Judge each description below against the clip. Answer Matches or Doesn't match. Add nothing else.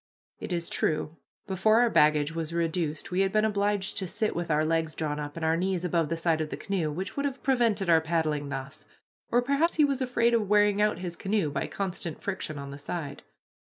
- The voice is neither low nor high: Matches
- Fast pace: Matches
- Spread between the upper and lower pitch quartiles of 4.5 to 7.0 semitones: Matches